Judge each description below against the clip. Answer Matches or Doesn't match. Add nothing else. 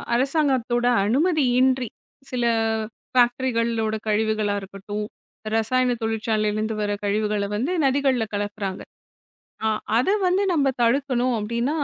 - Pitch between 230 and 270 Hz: Matches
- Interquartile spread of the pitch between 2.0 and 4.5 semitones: Matches